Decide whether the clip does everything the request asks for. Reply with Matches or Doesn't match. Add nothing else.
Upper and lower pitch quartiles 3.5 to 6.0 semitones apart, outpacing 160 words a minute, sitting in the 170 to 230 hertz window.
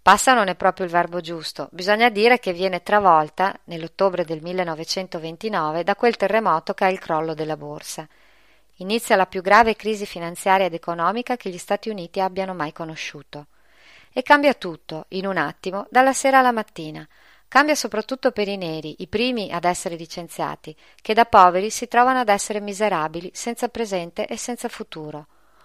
Matches